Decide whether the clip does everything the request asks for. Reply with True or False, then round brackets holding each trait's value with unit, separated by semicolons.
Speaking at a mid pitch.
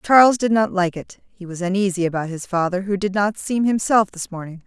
False (195 Hz)